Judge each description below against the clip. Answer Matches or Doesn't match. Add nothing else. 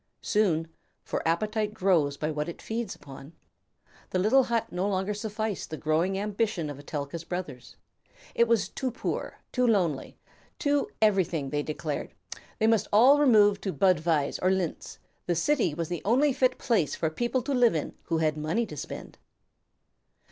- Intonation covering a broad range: Matches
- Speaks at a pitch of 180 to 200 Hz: Matches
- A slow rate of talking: Doesn't match